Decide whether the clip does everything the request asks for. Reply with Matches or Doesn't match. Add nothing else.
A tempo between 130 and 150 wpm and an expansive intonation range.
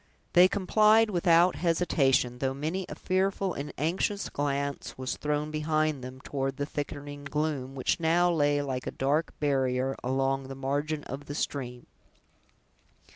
Doesn't match